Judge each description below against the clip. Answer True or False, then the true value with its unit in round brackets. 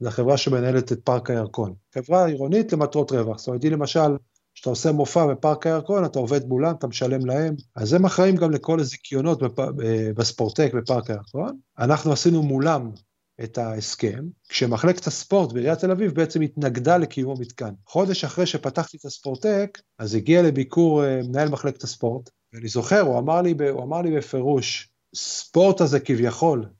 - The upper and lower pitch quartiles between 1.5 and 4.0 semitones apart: False (4.7 semitones)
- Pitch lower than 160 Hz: True (140 Hz)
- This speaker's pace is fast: True (160 wpm)